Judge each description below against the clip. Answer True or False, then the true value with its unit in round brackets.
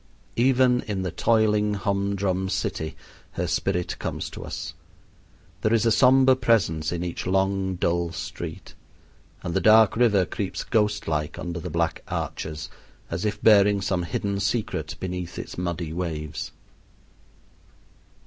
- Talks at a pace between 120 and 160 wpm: True (140 wpm)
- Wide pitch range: False (3.5 semitones)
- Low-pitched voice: True (95 Hz)